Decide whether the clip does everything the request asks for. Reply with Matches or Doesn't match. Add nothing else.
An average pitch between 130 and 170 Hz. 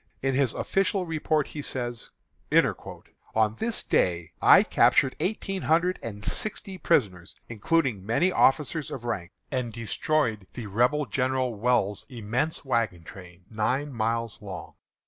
Doesn't match